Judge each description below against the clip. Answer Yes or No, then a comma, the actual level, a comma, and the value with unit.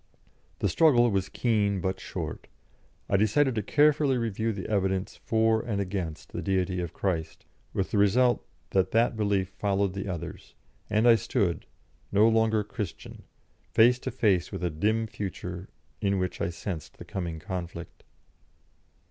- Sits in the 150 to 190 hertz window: No, low, 100 Hz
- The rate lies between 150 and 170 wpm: Yes, average, 155 wpm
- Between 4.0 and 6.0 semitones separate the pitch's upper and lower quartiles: No, average, 3.2 semitones